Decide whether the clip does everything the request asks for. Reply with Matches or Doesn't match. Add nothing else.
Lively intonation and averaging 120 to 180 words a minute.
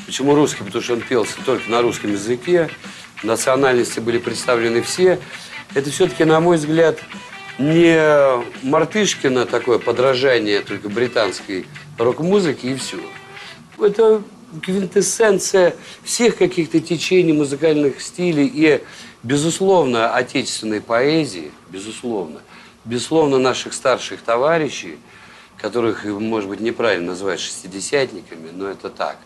Doesn't match